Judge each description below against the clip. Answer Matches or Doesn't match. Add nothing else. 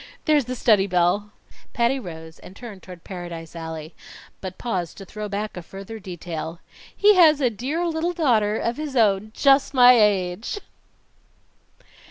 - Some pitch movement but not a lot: Doesn't match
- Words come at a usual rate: Matches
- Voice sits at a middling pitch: Doesn't match